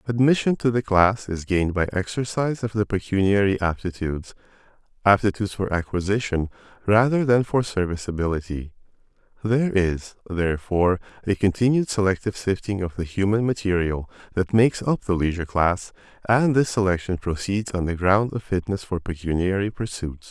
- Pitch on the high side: No, low, 100 Hz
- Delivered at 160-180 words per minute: No, average, 140 wpm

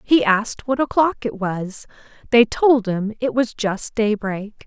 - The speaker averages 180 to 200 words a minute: No, average, 165 wpm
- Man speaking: No, female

